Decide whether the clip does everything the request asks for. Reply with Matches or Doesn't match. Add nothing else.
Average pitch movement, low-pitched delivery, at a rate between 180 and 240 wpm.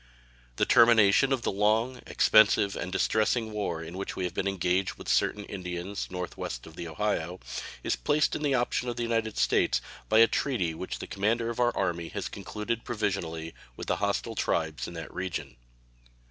Matches